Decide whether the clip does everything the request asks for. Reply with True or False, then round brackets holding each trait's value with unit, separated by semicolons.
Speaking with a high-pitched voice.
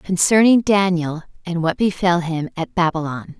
False (175 Hz)